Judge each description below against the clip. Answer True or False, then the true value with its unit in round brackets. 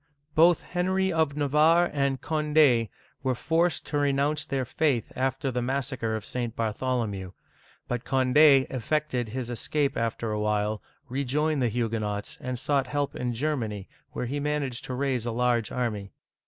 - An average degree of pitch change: True (4.1 semitones)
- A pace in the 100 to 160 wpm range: True (155 wpm)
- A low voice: True (130 Hz)